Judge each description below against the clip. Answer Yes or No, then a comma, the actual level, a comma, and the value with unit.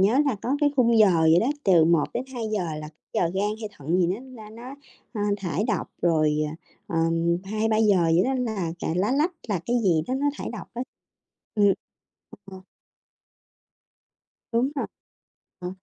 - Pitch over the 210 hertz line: No, high, 205 Hz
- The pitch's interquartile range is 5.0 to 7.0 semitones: Yes, wide, 5.6 semitones